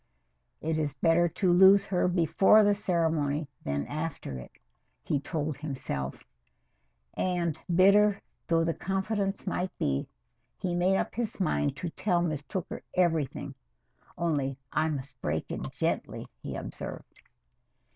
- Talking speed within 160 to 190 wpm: No, slow, 135 wpm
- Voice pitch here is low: No, medium, 165 Hz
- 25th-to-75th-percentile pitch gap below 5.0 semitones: Yes, average, 4.4 semitones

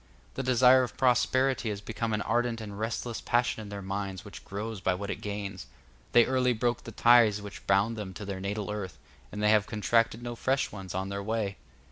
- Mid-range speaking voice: No, low, 105 Hz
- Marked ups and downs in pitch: No, average, 3.1 semitones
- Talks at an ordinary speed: No, fast, 210 wpm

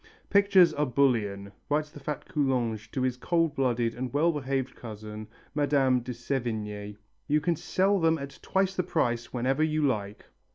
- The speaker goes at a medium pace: Yes, average, 165 wpm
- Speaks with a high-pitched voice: No, low, 135 Hz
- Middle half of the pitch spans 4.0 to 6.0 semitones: Yes, average, 4.6 semitones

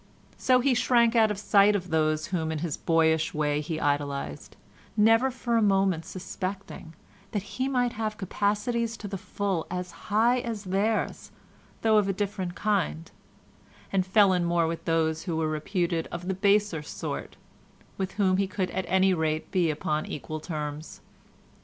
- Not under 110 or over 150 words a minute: No, average, 170 wpm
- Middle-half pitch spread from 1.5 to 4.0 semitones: No, average, 4.6 semitones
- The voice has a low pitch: No, high, 190 Hz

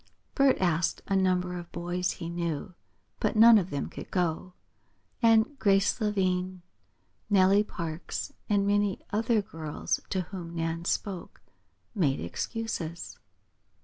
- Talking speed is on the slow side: Yes, slow, 125 wpm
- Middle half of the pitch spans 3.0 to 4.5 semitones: Yes, average, 3.3 semitones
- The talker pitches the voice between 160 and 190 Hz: Yes, medium, 185 Hz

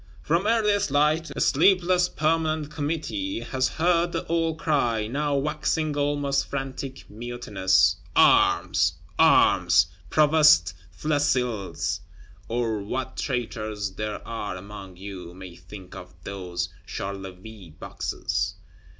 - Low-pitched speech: Yes, low, 130 Hz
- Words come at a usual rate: No, slow, 105 wpm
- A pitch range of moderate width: No, wide, 7.9 semitones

